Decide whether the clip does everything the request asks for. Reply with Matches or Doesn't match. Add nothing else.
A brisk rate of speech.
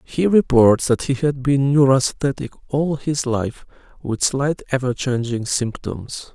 Doesn't match